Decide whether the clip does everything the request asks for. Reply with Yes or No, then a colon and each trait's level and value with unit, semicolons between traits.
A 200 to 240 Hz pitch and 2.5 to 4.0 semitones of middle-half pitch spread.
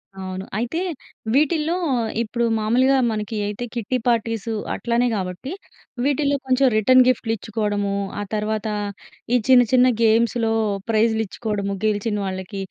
Yes: high, 225 Hz; average, 3.4 semitones